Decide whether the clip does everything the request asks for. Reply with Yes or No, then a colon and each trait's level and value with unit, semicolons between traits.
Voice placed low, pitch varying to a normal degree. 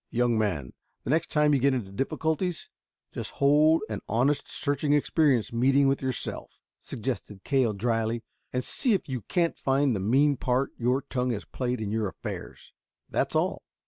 Yes: low, 130 Hz; average, 3.8 semitones